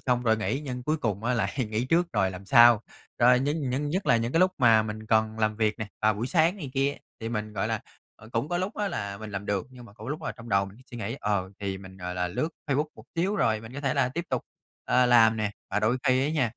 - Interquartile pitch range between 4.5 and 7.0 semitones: No, average, 4.1 semitones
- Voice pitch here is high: No, low, 115 Hz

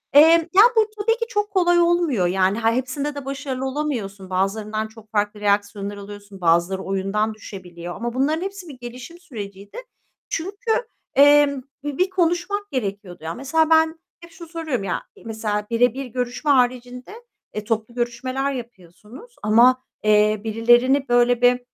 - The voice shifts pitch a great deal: Yes, wide, 6.5 semitones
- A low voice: No, high, 245 Hz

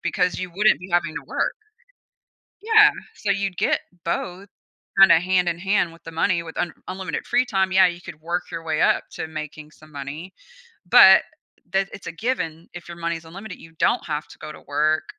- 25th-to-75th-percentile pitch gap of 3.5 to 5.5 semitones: No, average, 2.9 semitones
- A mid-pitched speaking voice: Yes, medium, 175 Hz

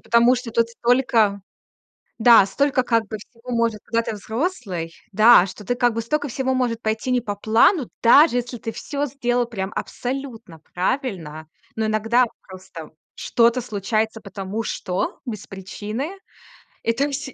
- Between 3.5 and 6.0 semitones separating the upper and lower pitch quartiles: No, average, 3.0 semitones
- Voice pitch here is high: Yes, high, 230 Hz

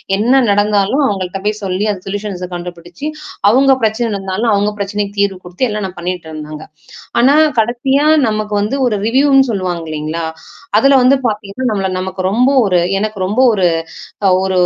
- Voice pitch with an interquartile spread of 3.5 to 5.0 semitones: Yes, average, 4.2 semitones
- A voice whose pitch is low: No, high, 205 Hz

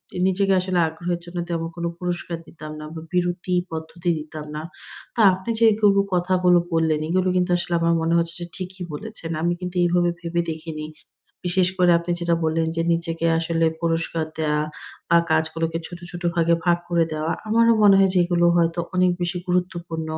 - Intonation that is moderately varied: No, narrow, 1.6 semitones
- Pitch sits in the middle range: Yes, medium, 175 Hz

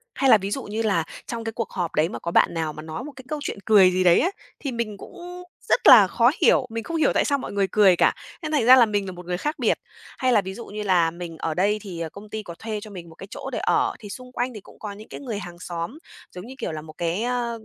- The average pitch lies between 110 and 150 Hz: No, high, 210 Hz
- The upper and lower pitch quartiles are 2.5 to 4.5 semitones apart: No, average, 5.2 semitones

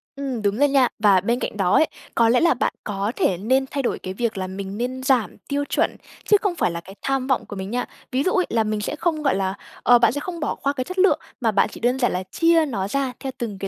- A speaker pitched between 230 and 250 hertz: Yes, high, 245 Hz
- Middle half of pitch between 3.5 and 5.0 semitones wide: No, wide, 5.5 semitones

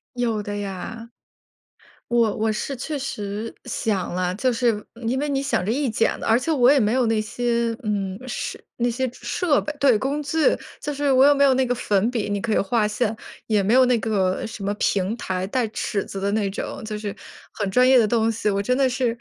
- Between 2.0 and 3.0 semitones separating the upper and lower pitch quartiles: No, average, 3.7 semitones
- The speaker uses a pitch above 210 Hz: Yes, high, 230 Hz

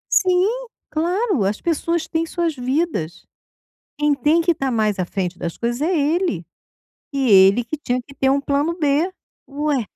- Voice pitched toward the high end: Yes, very high, 285 Hz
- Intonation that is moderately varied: No, wide, 5.8 semitones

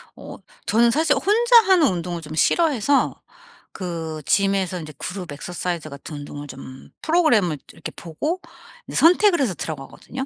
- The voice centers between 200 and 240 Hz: No, medium, 185 Hz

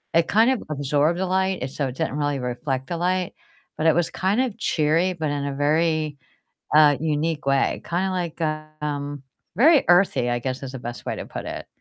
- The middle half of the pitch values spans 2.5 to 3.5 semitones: No, average, 4.1 semitones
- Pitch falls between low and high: Yes, medium, 155 Hz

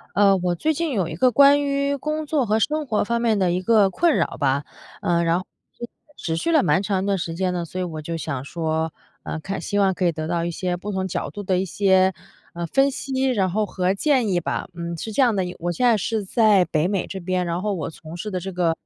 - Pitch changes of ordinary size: Yes, average, 4.7 semitones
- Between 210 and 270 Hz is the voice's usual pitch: No, high, 190 Hz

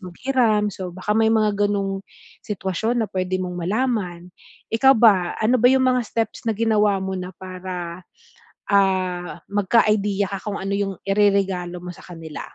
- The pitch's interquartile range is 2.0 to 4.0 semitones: Yes, average, 2.9 semitones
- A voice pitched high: Yes, high, 200 Hz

